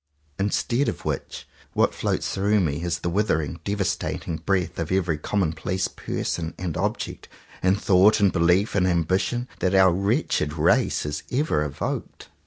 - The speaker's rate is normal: Yes, average, 155 wpm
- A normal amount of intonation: Yes, average, 3.3 semitones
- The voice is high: No, very low, 90 Hz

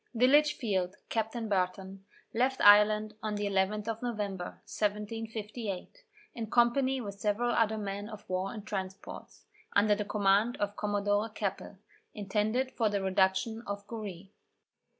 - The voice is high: Yes, high, 210 Hz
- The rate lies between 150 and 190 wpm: No, slow, 135 wpm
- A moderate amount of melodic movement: No, narrow, 2.1 semitones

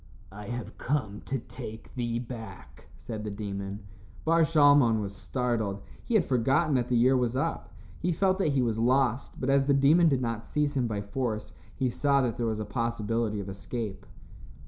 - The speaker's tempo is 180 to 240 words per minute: Yes, average, 190 wpm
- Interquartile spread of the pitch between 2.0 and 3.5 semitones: No, average, 4.3 semitones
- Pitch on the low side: Yes, low, 120 Hz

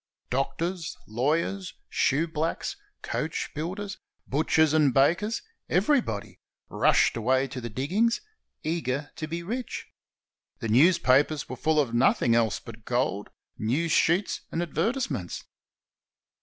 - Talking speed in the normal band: No, slow, 120 wpm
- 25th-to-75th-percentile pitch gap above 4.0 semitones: Yes, average, 5.2 semitones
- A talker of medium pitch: Yes, medium, 150 Hz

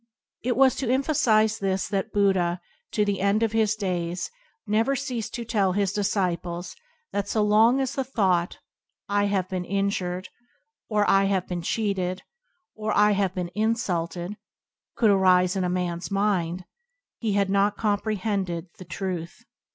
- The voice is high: Yes, high, 200 Hz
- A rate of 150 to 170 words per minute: Yes, average, 160 wpm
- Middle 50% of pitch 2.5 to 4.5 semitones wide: Yes, average, 2.9 semitones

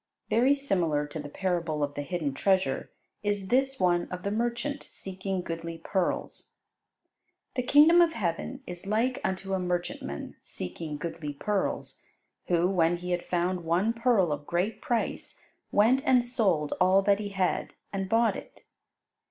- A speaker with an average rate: Yes, average, 155 wpm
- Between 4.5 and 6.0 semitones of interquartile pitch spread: Yes, average, 4.9 semitones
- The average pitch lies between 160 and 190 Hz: Yes, medium, 185 Hz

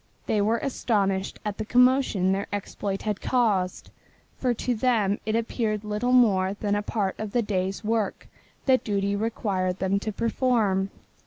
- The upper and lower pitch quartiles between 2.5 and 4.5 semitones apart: Yes, average, 2.8 semitones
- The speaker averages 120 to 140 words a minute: No, average, 160 wpm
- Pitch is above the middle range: Yes, high, 210 Hz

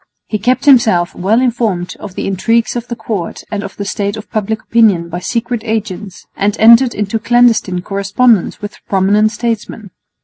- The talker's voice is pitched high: Yes, high, 215 Hz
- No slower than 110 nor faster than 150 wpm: No, average, 170 wpm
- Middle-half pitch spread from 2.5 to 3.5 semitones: Yes, average, 3.0 semitones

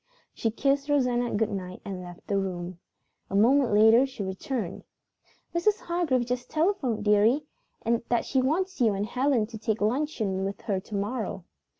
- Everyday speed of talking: Yes, average, 165 wpm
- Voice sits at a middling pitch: No, high, 225 Hz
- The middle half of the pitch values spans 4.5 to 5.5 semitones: Yes, average, 5.1 semitones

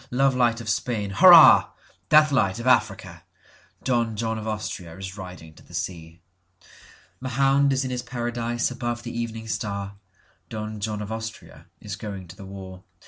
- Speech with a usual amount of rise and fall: Yes, average, 3.9 semitones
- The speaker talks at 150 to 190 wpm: No, average, 140 wpm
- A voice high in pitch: No, low, 110 Hz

